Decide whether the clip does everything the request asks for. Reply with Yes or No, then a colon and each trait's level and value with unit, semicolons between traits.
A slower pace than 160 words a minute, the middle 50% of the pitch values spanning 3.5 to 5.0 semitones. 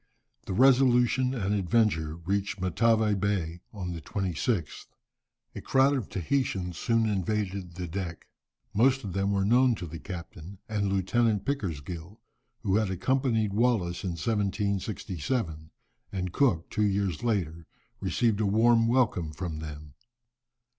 Yes: slow, 135 wpm; average, 4.6 semitones